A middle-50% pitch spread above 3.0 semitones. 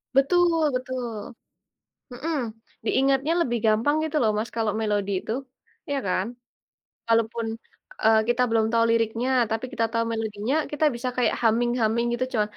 No: average, 2.7 semitones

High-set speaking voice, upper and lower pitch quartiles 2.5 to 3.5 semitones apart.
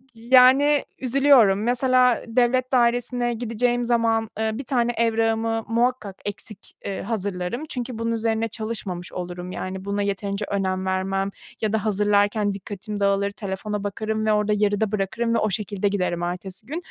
Yes: high, 215 Hz; average, 3.1 semitones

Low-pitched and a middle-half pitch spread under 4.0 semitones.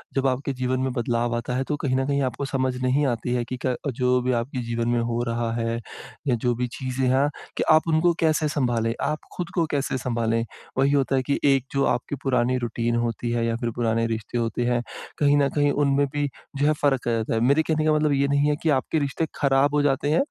Yes: low, 130 Hz; average, 3.1 semitones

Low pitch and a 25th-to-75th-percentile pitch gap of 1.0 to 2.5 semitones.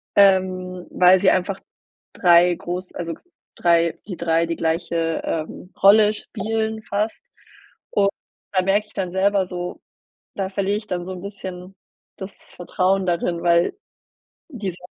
No: medium, 185 Hz; narrow, 2.2 semitones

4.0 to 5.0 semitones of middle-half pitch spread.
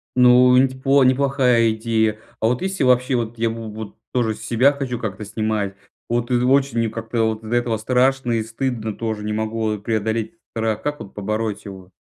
No: narrow, 2.5 semitones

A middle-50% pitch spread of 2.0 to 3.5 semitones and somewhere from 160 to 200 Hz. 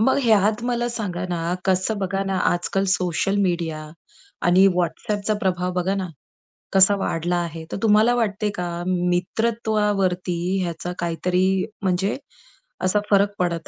Yes: average, 2.8 semitones; medium, 185 Hz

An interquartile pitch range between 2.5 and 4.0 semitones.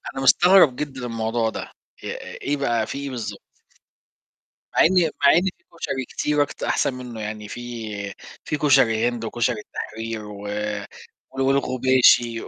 Yes: average, 3.7 semitones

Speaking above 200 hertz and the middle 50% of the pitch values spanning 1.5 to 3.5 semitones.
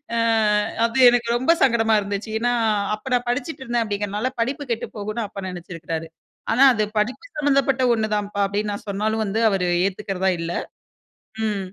Yes: high, 215 Hz; average, 3.2 semitones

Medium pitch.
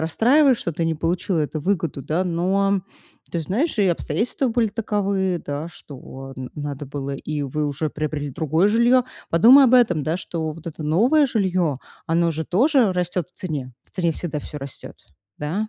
Yes: medium, 170 Hz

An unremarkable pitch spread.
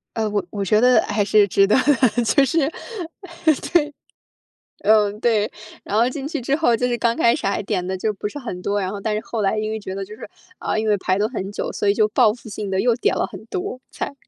Yes: average, 3.8 semitones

